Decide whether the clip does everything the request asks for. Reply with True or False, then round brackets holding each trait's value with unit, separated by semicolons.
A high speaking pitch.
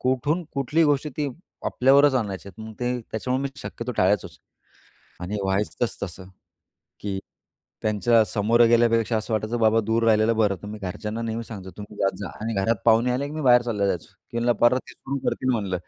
False (115 Hz)